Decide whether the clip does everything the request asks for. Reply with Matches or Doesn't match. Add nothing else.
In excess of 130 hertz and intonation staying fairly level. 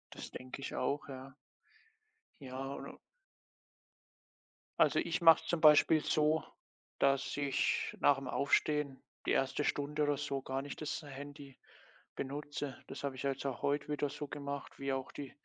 Matches